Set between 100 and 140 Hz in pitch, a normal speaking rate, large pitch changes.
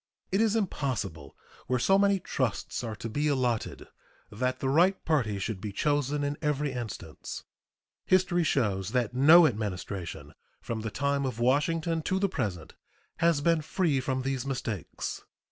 Yes: low, 135 Hz; average, 155 wpm; wide, 6.2 semitones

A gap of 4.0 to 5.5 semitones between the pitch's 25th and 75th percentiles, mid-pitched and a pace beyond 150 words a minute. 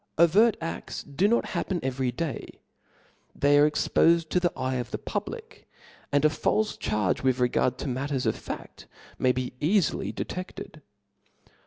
Yes: average, 4.8 semitones; medium, 145 Hz; average, 160 wpm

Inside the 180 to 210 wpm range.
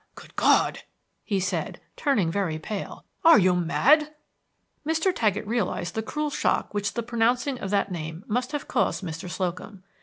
No: average, 160 wpm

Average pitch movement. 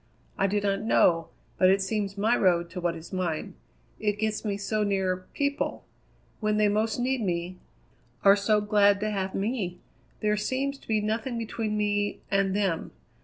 No: narrow, 2.1 semitones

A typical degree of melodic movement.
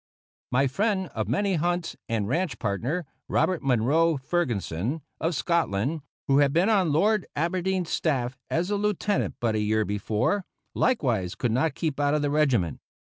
No: wide, 6.6 semitones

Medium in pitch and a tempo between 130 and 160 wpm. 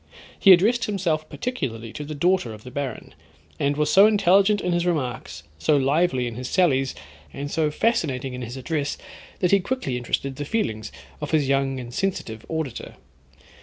No: medium, 145 Hz; average, 175 wpm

